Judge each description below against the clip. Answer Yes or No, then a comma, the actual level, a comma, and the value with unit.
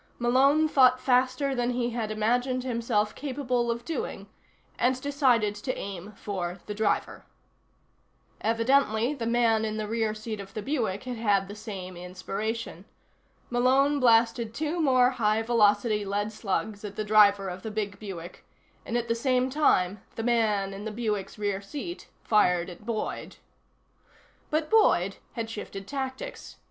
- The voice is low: No, high, 225 Hz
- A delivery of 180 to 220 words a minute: No, average, 155 wpm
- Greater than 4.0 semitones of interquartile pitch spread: No, average, 3.5 semitones